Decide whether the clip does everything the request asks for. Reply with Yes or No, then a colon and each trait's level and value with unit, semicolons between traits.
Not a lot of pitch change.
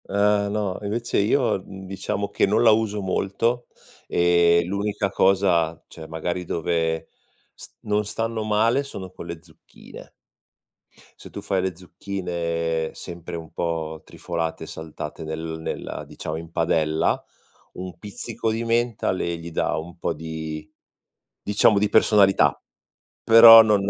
No: average, 4.0 semitones